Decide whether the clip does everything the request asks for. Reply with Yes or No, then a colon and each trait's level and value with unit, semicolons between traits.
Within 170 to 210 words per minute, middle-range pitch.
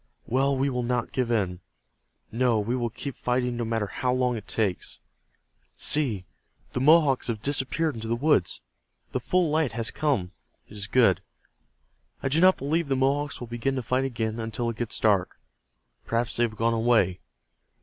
No: average, 180 wpm; low, 120 Hz